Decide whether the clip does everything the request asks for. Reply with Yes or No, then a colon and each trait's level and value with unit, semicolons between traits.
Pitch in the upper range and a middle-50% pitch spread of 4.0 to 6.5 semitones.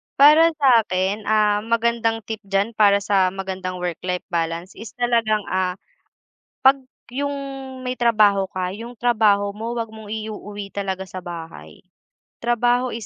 No: high, 210 Hz; average, 3.5 semitones